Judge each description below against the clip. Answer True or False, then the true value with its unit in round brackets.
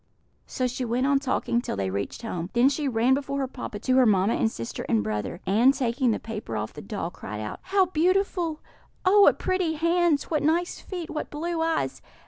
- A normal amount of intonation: False (7.2 semitones)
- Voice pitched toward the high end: True (260 Hz)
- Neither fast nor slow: False (210 wpm)